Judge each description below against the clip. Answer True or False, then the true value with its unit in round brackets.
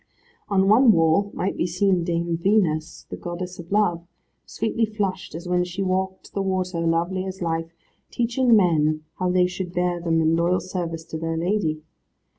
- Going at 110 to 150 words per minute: False (175 wpm)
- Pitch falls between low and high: True (180 Hz)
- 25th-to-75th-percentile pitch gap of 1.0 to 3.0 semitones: True (2.4 semitones)